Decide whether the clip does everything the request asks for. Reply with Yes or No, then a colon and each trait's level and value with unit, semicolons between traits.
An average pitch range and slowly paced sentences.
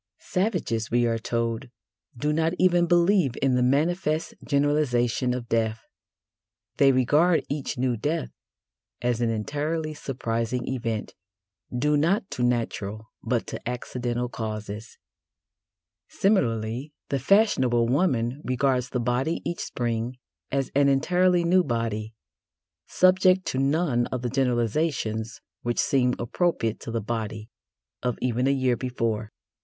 Yes: average, 4.4 semitones; slow, 130 wpm